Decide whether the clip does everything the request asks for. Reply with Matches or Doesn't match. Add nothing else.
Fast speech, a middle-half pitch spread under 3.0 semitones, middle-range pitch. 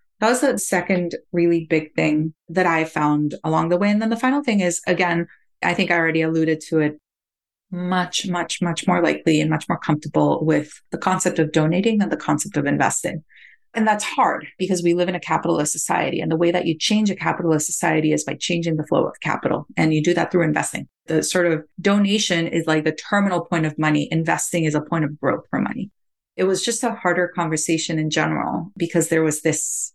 Matches